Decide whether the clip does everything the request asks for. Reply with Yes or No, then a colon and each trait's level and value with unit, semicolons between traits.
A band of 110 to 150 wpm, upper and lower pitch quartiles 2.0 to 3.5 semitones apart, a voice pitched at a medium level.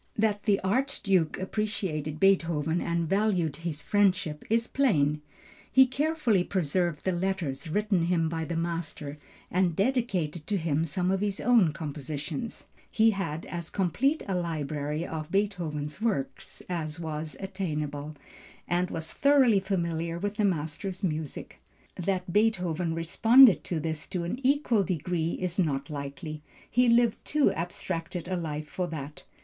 No: average, 145 wpm; average, 4.4 semitones; medium, 175 Hz